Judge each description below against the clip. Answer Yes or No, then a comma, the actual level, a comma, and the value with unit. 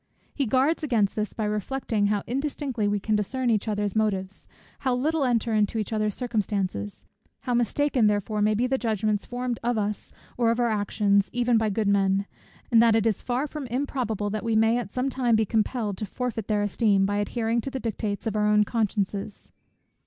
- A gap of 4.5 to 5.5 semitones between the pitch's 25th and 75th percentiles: No, average, 2.9 semitones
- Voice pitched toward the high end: Yes, high, 220 Hz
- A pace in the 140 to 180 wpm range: No, average, 200 wpm